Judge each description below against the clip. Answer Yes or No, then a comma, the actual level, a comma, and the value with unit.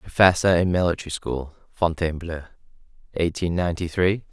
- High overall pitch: No, very low, 85 Hz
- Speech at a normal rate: No, slow, 110 wpm